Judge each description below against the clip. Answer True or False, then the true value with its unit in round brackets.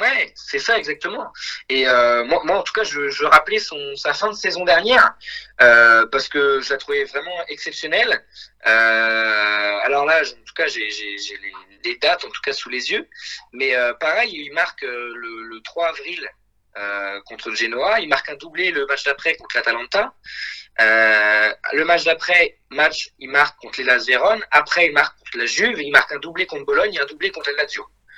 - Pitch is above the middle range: False (145 Hz)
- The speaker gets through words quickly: False (200 wpm)